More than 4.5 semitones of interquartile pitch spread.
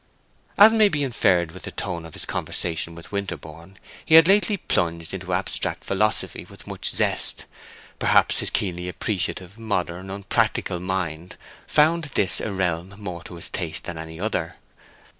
No: average, 4.0 semitones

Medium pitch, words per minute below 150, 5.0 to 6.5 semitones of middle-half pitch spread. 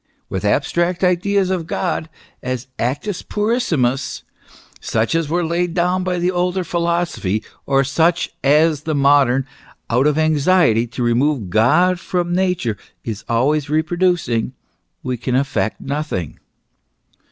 Yes: medium, 155 Hz; average, 140 wpm; wide, 5.6 semitones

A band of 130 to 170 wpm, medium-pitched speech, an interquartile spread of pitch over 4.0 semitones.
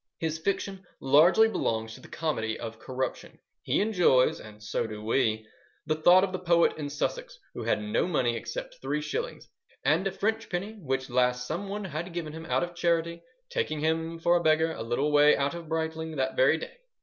No: average, 195 wpm; medium, 160 Hz; wide, 5.4 semitones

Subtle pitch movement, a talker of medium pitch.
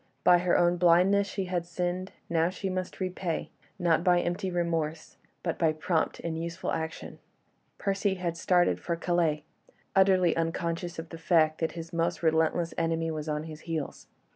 Yes: narrow, 1.7 semitones; medium, 170 Hz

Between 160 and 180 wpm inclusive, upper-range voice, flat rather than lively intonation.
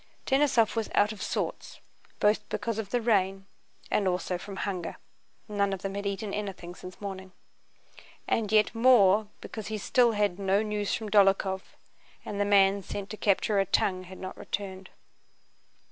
Yes: average, 165 wpm; high, 200 Hz; narrow, 1.9 semitones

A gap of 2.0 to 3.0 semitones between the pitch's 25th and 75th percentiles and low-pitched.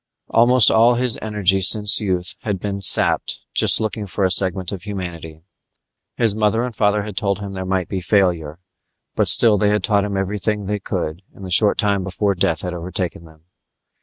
Yes: narrow, 2.4 semitones; low, 100 Hz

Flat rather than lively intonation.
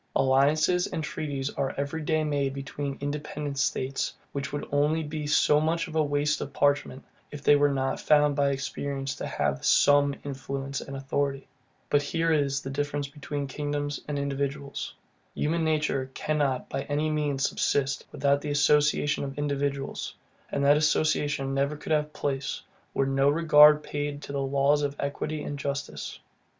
Yes: narrow, 1.3 semitones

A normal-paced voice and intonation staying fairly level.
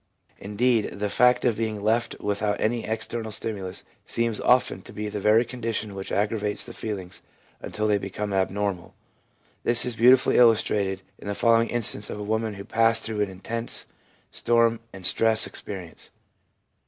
Yes: average, 160 wpm; narrow, 2.2 semitones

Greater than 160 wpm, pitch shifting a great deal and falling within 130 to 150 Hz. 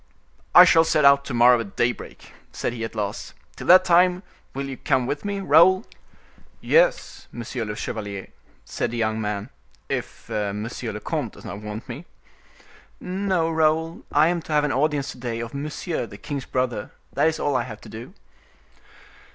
Yes: average, 185 wpm; wide, 6.1 semitones; low, 135 Hz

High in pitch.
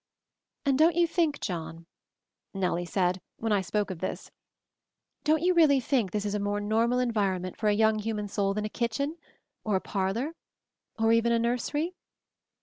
Yes: high, 220 Hz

